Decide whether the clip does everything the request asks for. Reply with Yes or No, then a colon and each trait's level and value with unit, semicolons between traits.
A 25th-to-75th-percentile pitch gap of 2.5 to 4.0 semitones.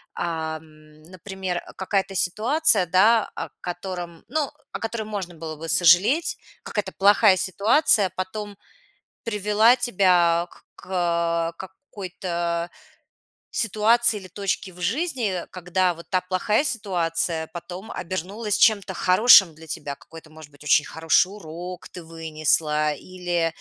Yes: average, 3.7 semitones